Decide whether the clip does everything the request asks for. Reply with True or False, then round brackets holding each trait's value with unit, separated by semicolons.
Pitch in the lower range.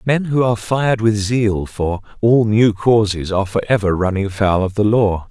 True (105 Hz)